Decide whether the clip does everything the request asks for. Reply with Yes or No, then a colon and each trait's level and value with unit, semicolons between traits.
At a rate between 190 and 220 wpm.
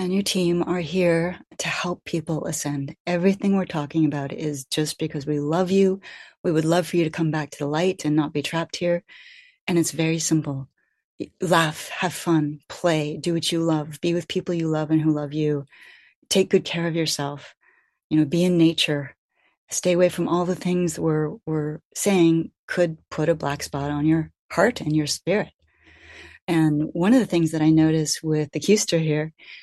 Yes: average, 200 wpm